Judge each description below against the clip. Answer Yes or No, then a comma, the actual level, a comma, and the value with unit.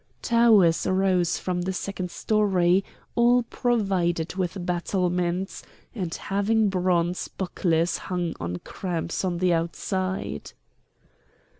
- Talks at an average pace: No, slow, 105 wpm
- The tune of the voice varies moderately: No, narrow, 2.2 semitones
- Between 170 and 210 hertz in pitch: Yes, medium, 185 Hz